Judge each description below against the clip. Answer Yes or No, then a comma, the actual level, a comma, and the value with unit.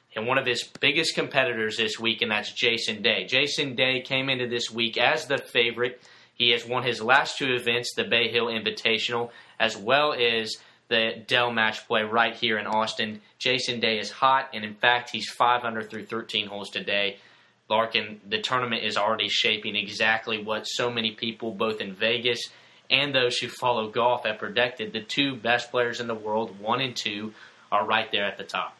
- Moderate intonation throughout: No, narrow, 2.0 semitones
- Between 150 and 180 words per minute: No, average, 195 wpm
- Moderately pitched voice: No, low, 115 Hz